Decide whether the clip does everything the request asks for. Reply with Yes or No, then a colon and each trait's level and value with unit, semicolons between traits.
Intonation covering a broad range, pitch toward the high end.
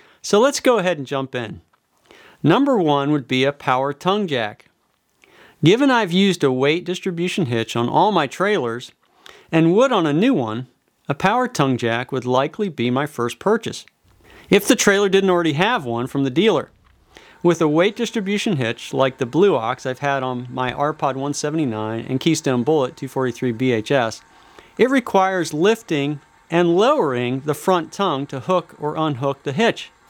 No: wide, 6.2 semitones; medium, 145 Hz